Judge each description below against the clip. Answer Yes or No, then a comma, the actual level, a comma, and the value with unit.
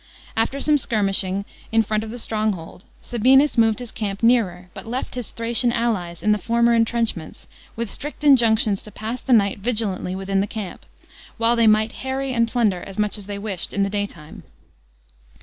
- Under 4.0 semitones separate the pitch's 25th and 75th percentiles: Yes, average, 2.9 semitones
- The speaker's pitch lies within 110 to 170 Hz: No, high, 220 Hz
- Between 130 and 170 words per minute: No, average, 185 wpm